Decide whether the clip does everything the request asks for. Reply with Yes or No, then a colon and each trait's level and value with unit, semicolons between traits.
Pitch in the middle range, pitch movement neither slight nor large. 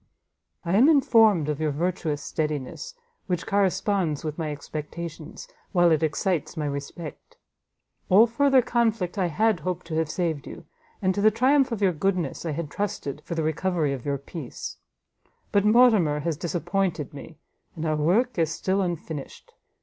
Yes: medium, 170 Hz; average, 4.7 semitones